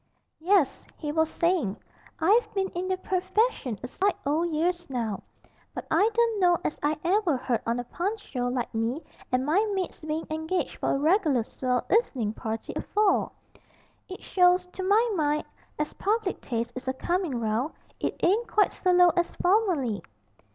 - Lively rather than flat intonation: Yes, wide, 6.7 semitones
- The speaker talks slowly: No, average, 170 wpm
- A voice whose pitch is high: Yes, very high, 335 Hz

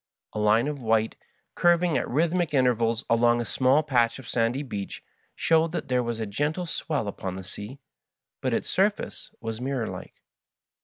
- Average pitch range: Yes, average, 4.7 semitones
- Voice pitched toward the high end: No, low, 125 Hz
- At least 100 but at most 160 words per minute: No, average, 170 wpm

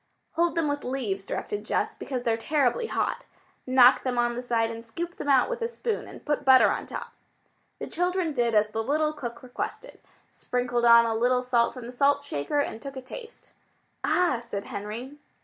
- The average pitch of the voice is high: Yes, very high, 255 Hz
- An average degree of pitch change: Yes, average, 4.0 semitones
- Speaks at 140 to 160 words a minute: No, average, 200 wpm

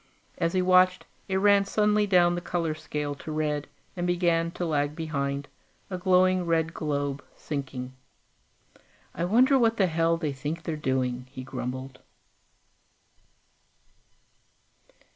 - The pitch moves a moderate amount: Yes, average, 4.2 semitones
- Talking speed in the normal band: No, slow, 130 wpm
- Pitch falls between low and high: Yes, medium, 165 Hz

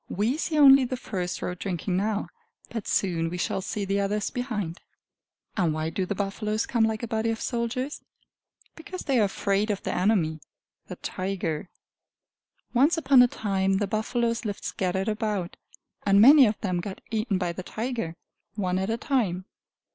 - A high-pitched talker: Yes, high, 205 Hz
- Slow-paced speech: No, average, 175 wpm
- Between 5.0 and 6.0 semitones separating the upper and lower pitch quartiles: No, average, 3.9 semitones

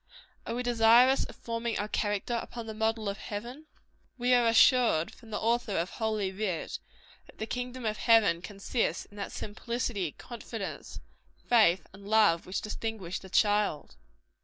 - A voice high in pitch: Yes, high, 220 Hz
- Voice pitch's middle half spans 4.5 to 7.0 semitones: No, average, 2.8 semitones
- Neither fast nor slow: Yes, average, 160 wpm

